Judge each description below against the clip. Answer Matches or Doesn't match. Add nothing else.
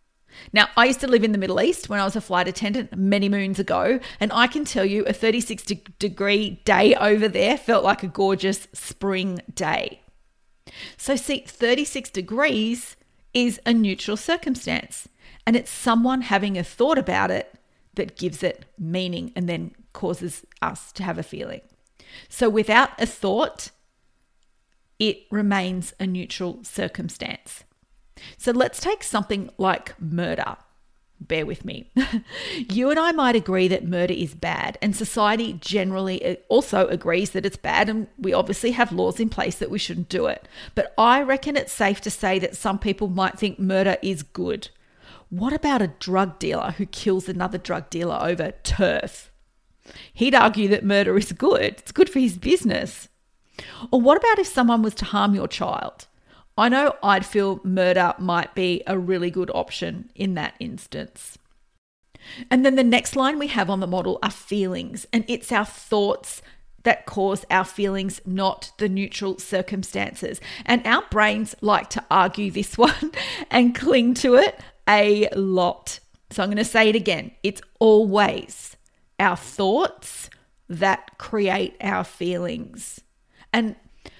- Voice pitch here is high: Matches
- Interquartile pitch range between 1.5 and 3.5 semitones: Doesn't match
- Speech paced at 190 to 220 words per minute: Doesn't match